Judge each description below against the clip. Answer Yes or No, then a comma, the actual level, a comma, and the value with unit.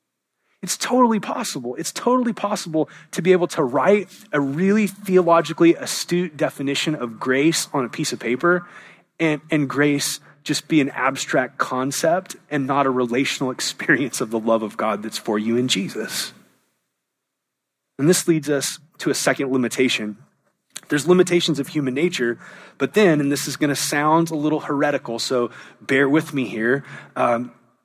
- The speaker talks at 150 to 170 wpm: Yes, average, 165 wpm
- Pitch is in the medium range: Yes, medium, 150 Hz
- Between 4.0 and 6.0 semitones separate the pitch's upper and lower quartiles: Yes, average, 4.9 semitones